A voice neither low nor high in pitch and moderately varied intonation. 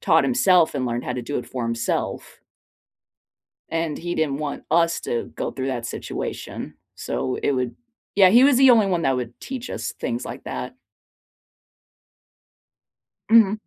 No: medium, 160 Hz; wide, 7.7 semitones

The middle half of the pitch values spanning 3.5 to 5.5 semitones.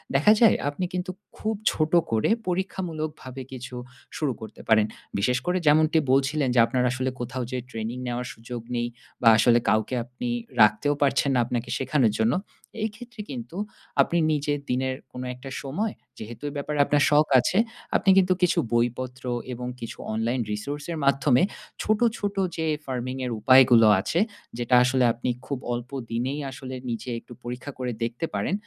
Yes: average, 3.8 semitones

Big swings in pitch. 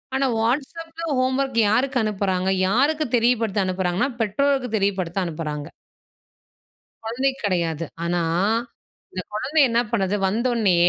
Yes: wide, 6.0 semitones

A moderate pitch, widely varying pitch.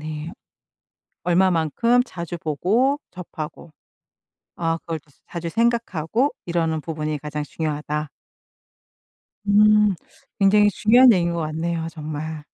No: medium, 170 Hz; average, 4.9 semitones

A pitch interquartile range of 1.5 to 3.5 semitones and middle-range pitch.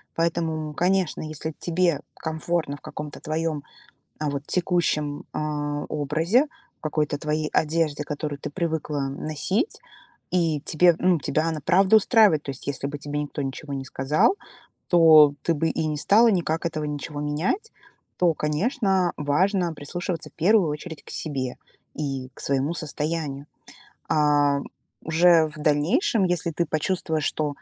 Yes: average, 2.8 semitones; medium, 155 Hz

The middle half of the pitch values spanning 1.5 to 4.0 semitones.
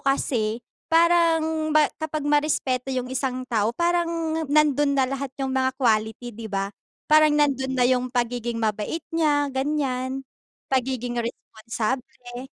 Yes: average, 3.4 semitones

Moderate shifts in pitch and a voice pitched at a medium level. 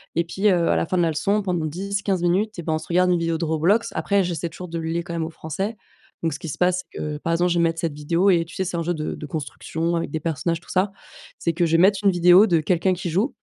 No: narrow, 2.3 semitones; medium, 170 Hz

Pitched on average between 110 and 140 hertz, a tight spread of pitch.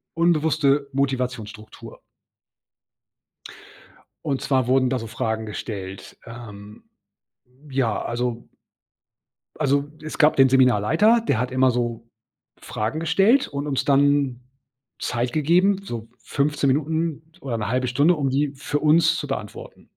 No: low, 135 Hz; average, 4.2 semitones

